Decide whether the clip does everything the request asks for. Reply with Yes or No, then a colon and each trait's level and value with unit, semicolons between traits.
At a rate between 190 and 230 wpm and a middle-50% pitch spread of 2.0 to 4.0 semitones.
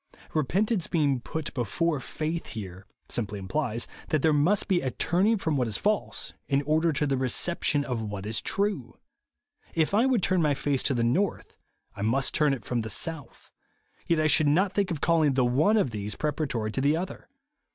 No: average, 200 wpm; wide, 5.6 semitones